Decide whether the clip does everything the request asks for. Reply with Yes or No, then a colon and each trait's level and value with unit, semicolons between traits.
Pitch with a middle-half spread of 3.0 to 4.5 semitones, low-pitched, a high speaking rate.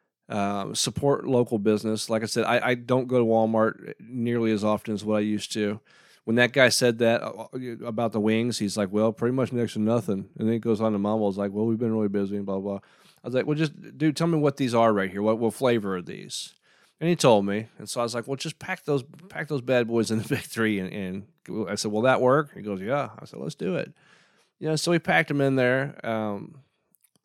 Yes: average, 3.3 semitones; low, 115 Hz; fast, 260 wpm